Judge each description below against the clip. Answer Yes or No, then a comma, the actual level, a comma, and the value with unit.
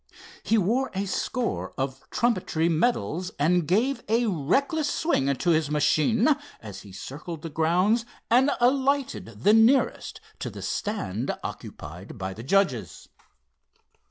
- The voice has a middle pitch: Yes, medium, 180 Hz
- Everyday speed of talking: No, slow, 130 wpm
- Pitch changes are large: Yes, wide, 9.0 semitones